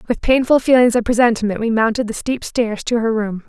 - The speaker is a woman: Yes, female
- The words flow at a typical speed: No, fast, 225 wpm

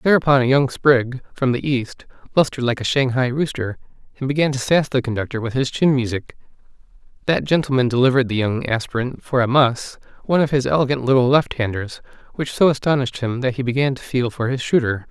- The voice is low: Yes, low, 130 Hz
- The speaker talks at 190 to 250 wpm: Yes, average, 200 wpm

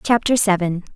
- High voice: Yes, high, 200 Hz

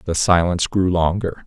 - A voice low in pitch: Yes, very low, 90 Hz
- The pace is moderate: Yes, average, 165 wpm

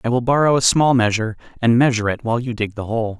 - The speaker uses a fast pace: Yes, fast, 265 wpm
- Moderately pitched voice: No, low, 120 Hz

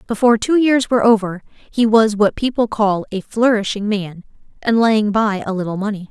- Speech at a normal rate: Yes, average, 185 wpm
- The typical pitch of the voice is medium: No, high, 215 Hz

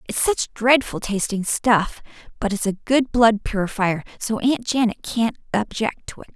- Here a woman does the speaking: Yes, female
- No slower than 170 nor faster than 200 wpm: No, average, 160 wpm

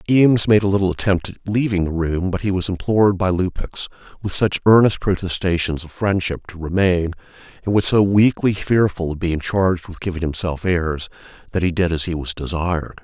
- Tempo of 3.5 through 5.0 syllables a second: No, 5.5 syllables/s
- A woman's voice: No, male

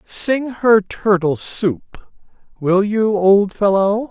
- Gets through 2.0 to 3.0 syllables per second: Yes, 2.8 syllables/s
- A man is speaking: Yes, male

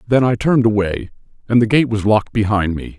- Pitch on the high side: No, low, 110 Hz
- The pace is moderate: No, fast, 220 wpm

